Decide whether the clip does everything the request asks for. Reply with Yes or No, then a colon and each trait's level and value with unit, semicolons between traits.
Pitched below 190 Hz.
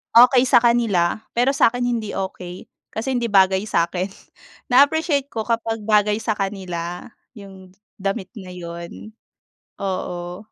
No: high, 210 Hz